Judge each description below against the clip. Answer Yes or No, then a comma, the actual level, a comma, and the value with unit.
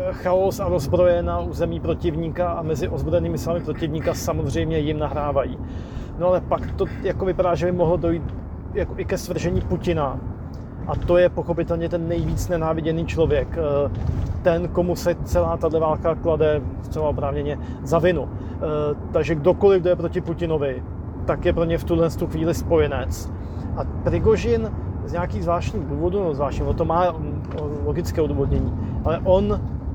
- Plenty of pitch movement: Yes, wide, 8.5 semitones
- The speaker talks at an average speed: Yes, average, 155 wpm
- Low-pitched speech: No, medium, 160 Hz